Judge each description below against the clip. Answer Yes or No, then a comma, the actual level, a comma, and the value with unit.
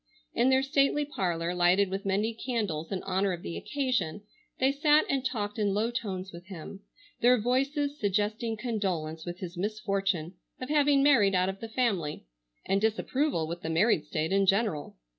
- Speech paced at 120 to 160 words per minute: No, average, 175 wpm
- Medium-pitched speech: No, high, 205 Hz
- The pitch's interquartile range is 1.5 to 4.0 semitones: No, wide, 5.5 semitones